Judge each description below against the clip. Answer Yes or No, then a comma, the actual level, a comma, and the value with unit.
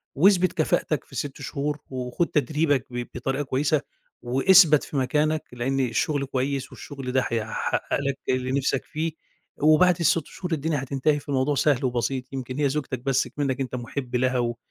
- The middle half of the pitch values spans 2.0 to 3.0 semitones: Yes, average, 2.7 semitones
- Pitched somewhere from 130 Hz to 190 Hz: Yes, low, 135 Hz